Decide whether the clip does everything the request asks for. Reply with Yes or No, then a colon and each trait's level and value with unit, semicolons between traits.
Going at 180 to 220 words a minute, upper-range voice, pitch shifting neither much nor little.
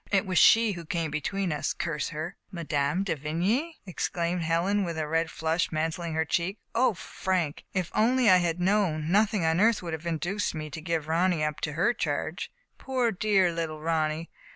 No: fast, 205 wpm; medium, 170 Hz; average, 3.6 semitones